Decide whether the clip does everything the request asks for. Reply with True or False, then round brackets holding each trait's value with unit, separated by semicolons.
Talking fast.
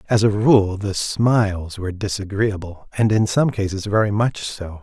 False (175 wpm)